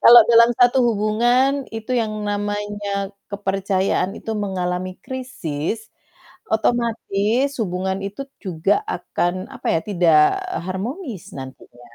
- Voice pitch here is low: No, high, 205 Hz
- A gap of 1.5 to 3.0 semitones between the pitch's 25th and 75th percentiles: No, average, 4.0 semitones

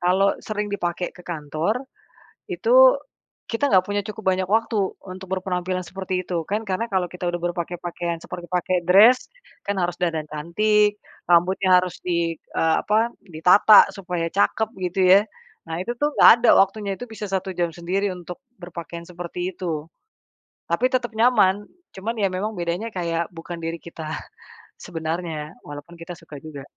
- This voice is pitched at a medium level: Yes, medium, 180 Hz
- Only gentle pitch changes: No, average, 3.1 semitones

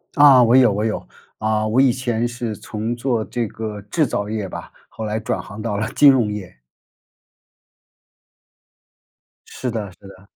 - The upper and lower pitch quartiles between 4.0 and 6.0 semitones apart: No, average, 2.7 semitones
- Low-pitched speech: Yes, low, 110 Hz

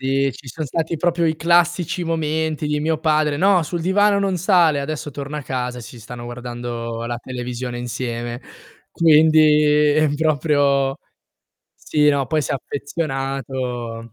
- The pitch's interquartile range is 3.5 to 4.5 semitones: Yes, average, 4.2 semitones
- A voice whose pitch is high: No, medium, 145 Hz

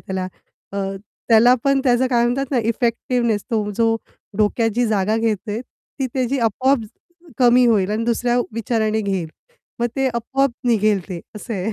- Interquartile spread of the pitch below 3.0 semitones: Yes, narrow, 2.5 semitones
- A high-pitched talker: Yes, high, 230 Hz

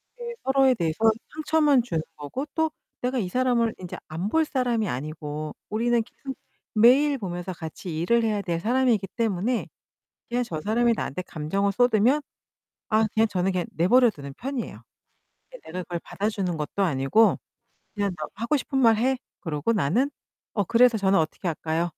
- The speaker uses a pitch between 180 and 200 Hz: No, high, 215 Hz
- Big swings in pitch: Yes, wide, 6.1 semitones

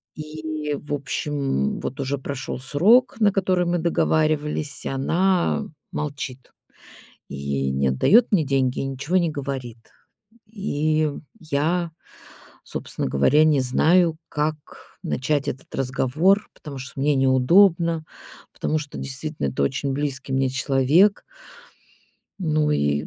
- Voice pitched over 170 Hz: No, medium, 145 Hz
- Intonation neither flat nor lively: Yes, average, 3.4 semitones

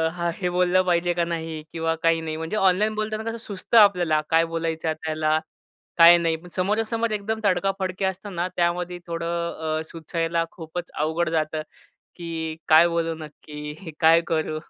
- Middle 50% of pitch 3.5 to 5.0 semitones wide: No, narrow, 2.4 semitones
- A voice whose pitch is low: No, medium, 170 Hz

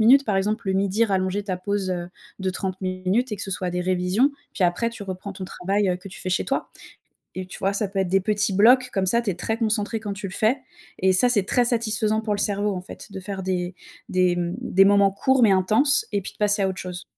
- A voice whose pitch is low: No, high, 195 Hz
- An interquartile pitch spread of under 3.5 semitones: Yes, narrow, 2.5 semitones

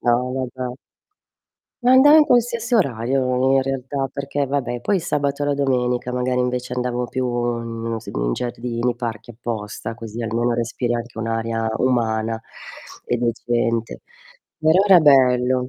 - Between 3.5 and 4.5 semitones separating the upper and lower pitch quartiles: No, narrow, 2.6 semitones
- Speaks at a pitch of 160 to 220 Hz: No, low, 125 Hz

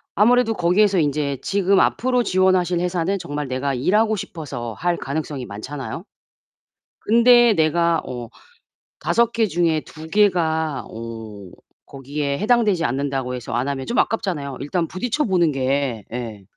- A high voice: No, medium, 160 Hz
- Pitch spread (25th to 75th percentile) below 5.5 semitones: No, wide, 6.4 semitones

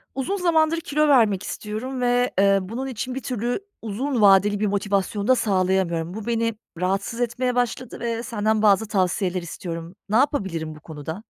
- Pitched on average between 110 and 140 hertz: No, high, 215 Hz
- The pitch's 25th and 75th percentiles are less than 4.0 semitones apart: No, average, 4.3 semitones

